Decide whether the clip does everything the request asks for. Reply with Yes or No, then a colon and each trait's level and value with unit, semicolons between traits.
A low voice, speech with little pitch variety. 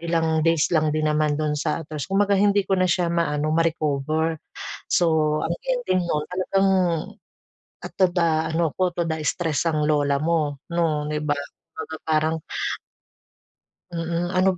No: medium, 160 Hz; narrow, 2.3 semitones